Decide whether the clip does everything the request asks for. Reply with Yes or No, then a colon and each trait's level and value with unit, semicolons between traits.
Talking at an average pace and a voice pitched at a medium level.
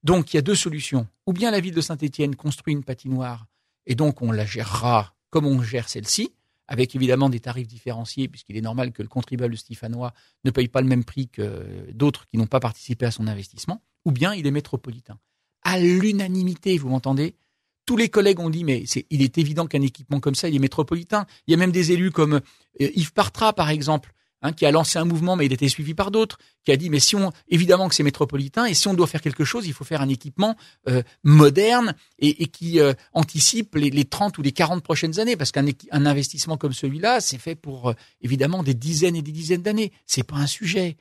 No: fast, 235 wpm; medium, 145 Hz